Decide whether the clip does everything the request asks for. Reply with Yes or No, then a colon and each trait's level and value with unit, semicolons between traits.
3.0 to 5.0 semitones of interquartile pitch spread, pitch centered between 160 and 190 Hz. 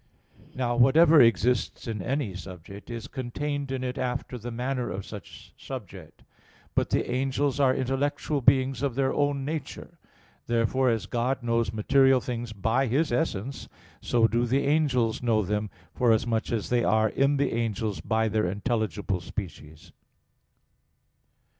No: average, 3.3 semitones; low, 120 Hz